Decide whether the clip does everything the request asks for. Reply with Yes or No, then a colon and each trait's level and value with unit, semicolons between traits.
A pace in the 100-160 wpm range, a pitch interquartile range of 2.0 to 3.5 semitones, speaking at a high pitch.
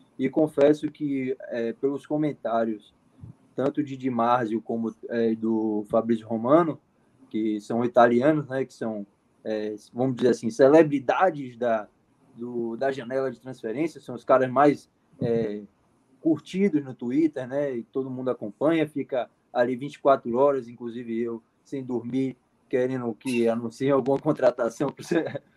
No: average, 140 wpm; average, 3.1 semitones; low, 130 Hz